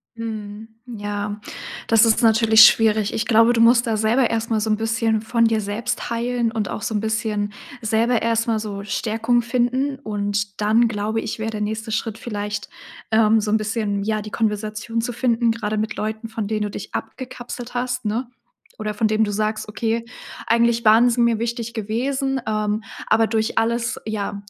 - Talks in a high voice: Yes, high, 220 Hz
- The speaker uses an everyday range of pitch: No, narrow, 1.6 semitones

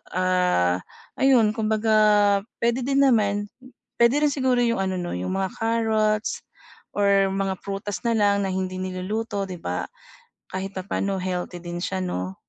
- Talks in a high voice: Yes, high, 200 Hz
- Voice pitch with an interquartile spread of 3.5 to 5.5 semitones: No, average, 3.1 semitones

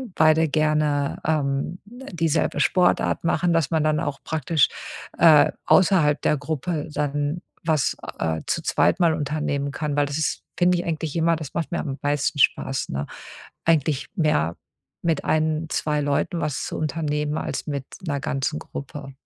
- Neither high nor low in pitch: Yes, medium, 155 Hz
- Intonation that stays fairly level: Yes, narrow, 2.2 semitones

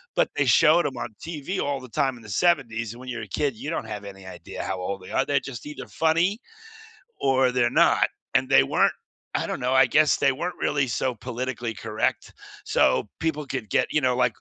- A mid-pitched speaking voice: No, low, 130 Hz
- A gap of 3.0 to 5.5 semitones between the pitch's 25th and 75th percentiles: Yes, average, 4.5 semitones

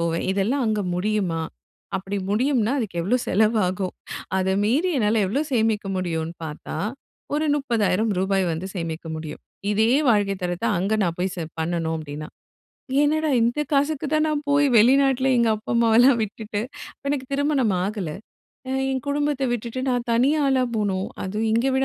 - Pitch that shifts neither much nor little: No, wide, 5.9 semitones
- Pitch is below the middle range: No, high, 215 Hz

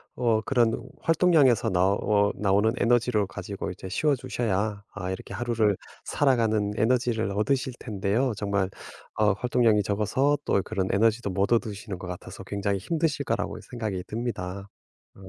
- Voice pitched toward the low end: Yes, low, 110 Hz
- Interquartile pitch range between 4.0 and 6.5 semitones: No, average, 3.4 semitones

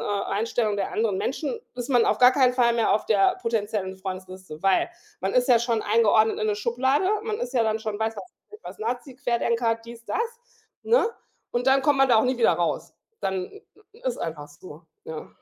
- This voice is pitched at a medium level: No, high, 230 Hz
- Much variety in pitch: No, average, 3.8 semitones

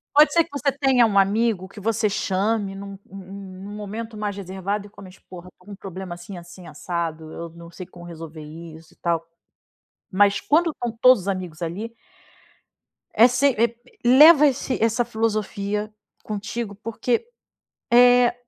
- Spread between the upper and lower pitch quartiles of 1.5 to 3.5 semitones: No, average, 4.1 semitones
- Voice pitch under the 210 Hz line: Yes, high, 200 Hz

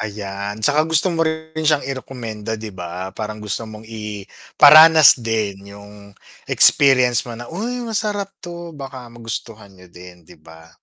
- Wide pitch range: Yes, wide, 7.3 semitones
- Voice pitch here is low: Yes, low, 115 Hz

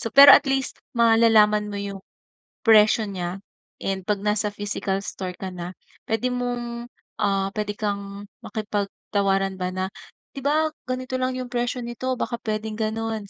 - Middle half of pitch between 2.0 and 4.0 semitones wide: Yes, average, 3.3 semitones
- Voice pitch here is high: Yes, high, 215 Hz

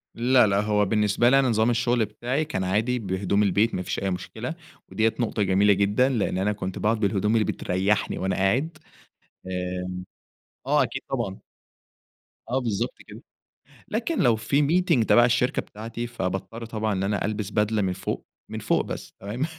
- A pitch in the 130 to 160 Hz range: No, low, 105 Hz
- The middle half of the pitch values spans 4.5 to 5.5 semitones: No, average, 3.6 semitones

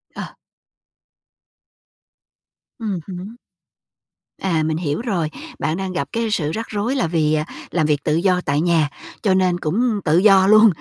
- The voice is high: No, medium, 180 Hz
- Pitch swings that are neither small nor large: Yes, average, 4.9 semitones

